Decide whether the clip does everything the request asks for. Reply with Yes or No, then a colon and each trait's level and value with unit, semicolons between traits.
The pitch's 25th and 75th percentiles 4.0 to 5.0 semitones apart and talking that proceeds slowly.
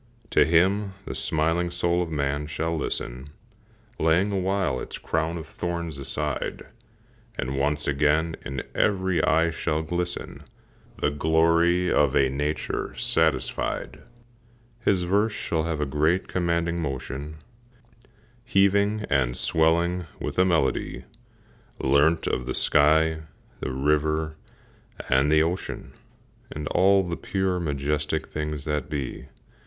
No: average, 2.9 semitones; slow, 125 wpm